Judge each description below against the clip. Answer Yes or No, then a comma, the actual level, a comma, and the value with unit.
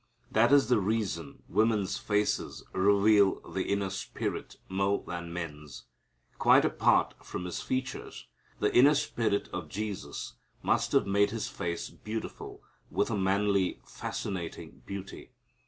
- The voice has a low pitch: Yes, low, 100 Hz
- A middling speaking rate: No, slow, 130 wpm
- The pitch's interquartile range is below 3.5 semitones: Yes, average, 2.7 semitones